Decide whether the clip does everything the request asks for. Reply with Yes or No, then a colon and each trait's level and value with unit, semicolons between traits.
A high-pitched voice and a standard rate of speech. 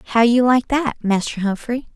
Yes: high, 235 Hz; average, 185 wpm